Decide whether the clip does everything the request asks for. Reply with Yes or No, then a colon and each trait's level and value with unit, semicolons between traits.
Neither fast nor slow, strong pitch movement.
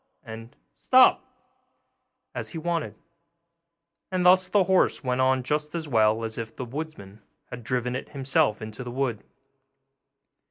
Yes: average, 145 wpm; wide, 5.7 semitones